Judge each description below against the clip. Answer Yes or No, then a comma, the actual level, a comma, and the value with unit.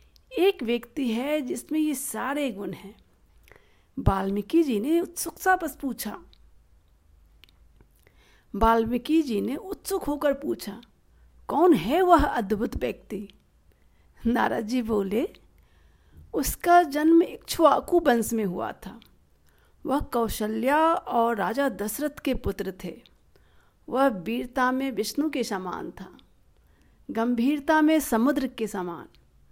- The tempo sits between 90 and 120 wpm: Yes, average, 115 wpm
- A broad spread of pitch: Yes, wide, 6.5 semitones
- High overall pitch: Yes, high, 245 Hz